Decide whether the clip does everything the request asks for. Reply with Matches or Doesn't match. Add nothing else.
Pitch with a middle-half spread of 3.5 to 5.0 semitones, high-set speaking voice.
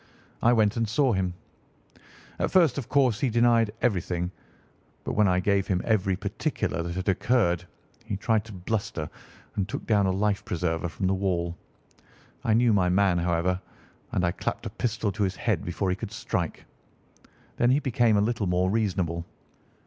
Doesn't match